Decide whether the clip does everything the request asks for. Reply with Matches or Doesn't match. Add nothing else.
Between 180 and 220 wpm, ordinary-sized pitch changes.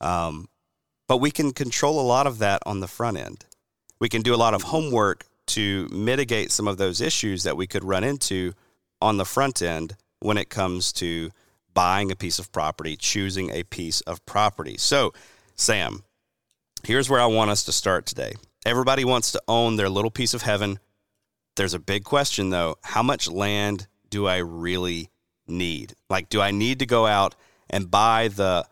Matches